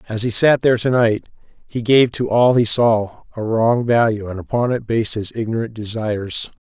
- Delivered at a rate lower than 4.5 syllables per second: No, 5.1 syllables/s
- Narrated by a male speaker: Yes, male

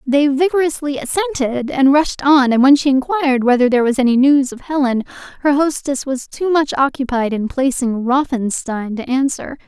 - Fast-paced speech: No, average, 175 wpm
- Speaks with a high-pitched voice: Yes, very high, 270 Hz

